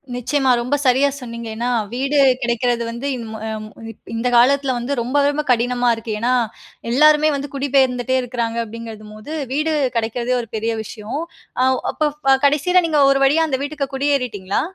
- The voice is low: No, very high, 250 Hz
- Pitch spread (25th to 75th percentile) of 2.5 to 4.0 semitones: Yes, average, 3.3 semitones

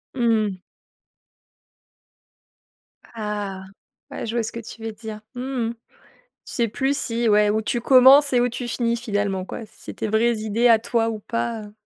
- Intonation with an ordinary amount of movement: No, narrow, 2.1 semitones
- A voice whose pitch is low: No, high, 230 Hz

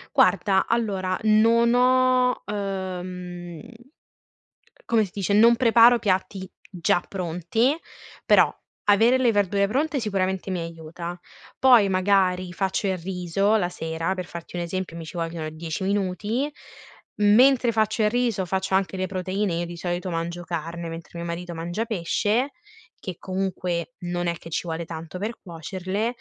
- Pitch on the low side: No, high, 190 Hz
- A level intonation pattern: No, average, 3.7 semitones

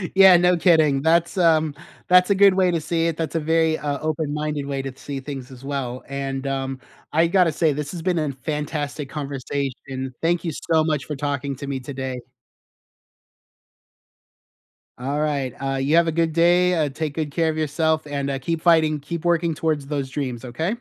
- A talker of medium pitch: Yes, medium, 150 Hz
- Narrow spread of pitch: No, average, 3.1 semitones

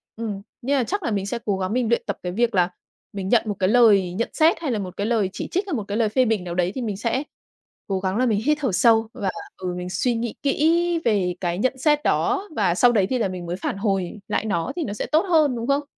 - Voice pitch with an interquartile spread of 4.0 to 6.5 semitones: Yes, average, 5.2 semitones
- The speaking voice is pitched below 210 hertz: No, high, 220 Hz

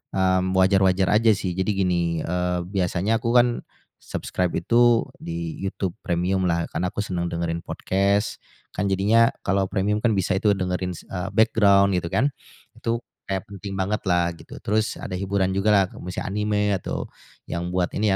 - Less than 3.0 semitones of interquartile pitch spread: Yes, narrow, 2.4 semitones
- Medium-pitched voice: No, very low, 95 Hz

